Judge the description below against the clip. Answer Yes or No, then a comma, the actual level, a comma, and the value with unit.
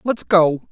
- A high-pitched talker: No, medium, 180 Hz